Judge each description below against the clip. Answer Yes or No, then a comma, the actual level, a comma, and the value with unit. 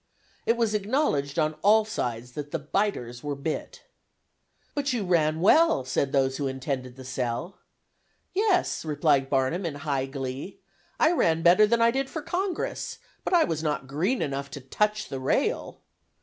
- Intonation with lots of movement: Yes, wide, 7.9 semitones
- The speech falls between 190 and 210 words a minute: No, average, 165 wpm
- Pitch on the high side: No, medium, 155 Hz